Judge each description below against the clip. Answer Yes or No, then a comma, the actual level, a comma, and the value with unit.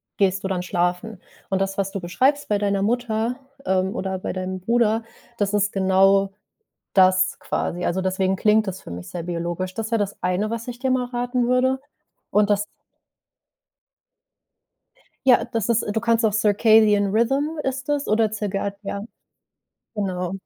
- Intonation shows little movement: No, average, 3.4 semitones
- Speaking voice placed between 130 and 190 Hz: No, high, 205 Hz